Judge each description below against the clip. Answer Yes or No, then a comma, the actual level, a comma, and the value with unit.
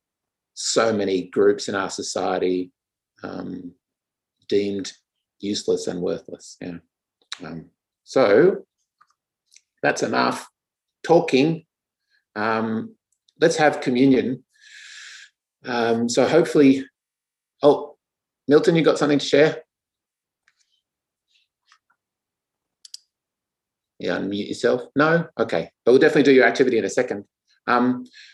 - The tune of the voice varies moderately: No, wide, 6.3 semitones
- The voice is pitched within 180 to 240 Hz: No, low, 135 Hz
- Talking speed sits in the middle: No, slow, 95 wpm